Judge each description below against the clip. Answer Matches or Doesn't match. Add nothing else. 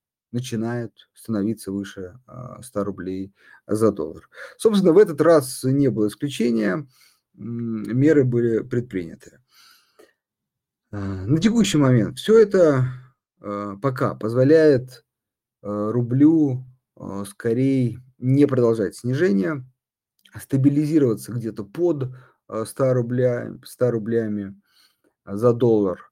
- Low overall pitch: Matches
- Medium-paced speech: Doesn't match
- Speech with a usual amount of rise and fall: Matches